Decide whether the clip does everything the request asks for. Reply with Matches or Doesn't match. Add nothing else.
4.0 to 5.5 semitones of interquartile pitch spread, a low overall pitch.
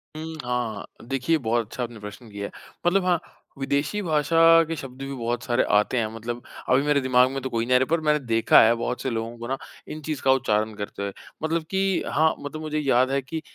Matches